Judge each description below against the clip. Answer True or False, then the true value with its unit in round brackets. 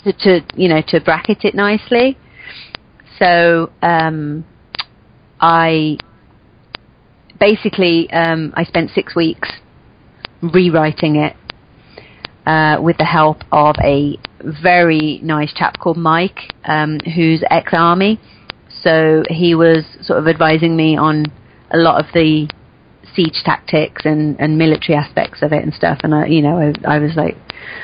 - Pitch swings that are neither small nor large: False (1.9 semitones)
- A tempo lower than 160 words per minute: True (135 wpm)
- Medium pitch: True (160 Hz)